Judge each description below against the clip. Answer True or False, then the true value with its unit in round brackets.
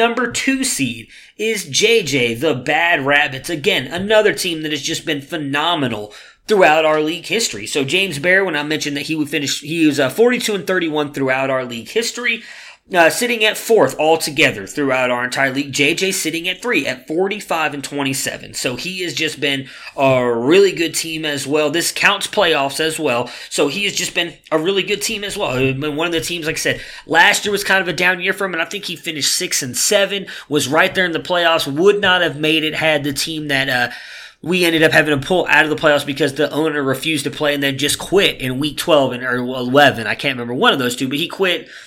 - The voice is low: False (155 Hz)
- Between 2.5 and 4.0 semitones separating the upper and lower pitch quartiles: False (4.5 semitones)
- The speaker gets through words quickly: True (230 wpm)